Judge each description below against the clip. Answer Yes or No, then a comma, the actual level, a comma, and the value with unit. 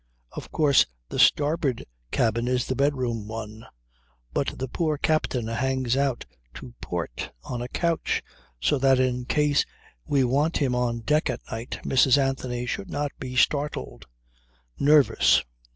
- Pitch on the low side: Yes, low, 130 Hz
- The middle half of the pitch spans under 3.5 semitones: Yes, average, 3.1 semitones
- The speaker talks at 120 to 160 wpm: Yes, average, 145 wpm